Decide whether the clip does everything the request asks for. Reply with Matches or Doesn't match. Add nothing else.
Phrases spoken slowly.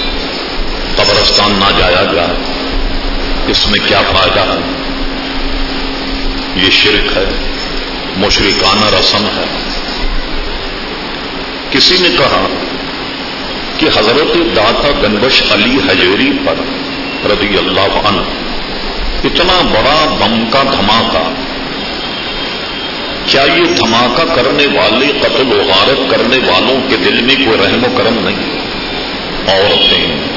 Matches